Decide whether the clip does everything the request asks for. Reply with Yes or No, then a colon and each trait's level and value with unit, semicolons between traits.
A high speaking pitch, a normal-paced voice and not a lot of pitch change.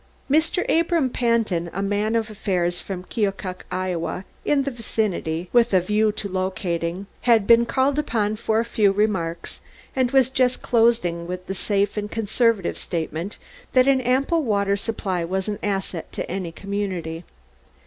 No: high, 205 Hz; average, 160 wpm; average, 4.2 semitones